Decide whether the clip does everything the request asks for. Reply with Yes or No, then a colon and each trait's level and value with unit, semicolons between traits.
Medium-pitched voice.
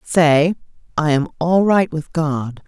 Yes: medium, 160 Hz